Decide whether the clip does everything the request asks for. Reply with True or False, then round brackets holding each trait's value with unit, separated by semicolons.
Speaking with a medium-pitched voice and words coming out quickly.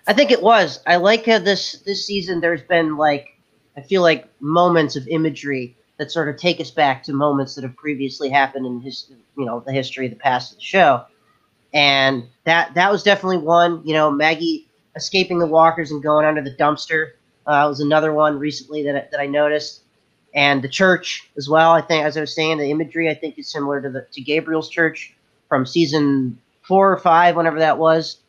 True (155 Hz; 210 wpm)